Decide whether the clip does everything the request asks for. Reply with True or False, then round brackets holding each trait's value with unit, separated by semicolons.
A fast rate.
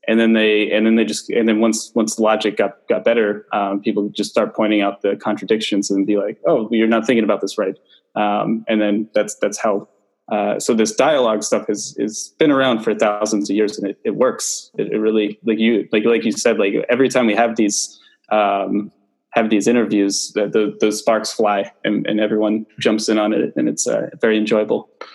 True (220 wpm)